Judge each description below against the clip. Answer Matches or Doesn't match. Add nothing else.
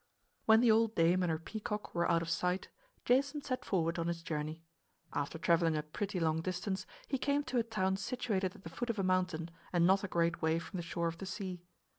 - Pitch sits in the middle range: Matches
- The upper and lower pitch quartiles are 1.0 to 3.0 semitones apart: Doesn't match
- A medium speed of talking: Doesn't match